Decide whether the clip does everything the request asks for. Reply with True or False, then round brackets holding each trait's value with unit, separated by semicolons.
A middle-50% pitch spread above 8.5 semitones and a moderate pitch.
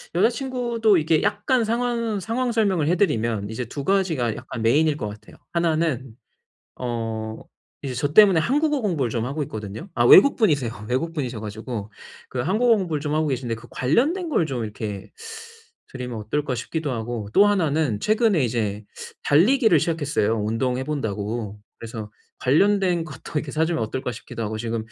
True (9.0 semitones; 145 Hz)